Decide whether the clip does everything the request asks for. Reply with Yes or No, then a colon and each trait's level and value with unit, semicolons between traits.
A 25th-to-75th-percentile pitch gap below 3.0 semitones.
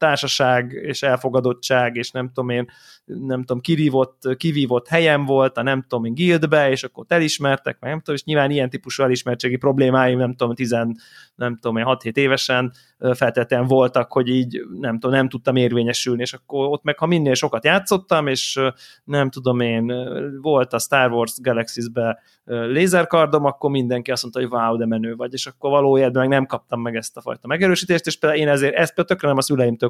Yes: narrow, 2.6 semitones